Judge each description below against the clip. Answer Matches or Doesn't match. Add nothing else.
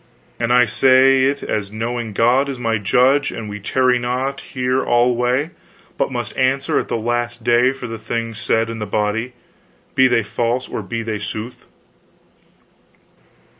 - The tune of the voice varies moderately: Doesn't match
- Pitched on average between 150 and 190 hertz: Doesn't match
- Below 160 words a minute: Doesn't match